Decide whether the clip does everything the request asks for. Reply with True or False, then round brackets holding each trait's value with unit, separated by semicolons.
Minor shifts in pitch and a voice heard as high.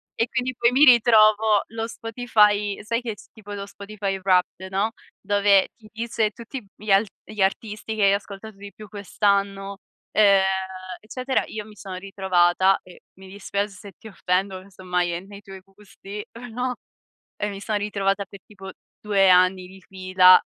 True (1.9 semitones; 200 Hz)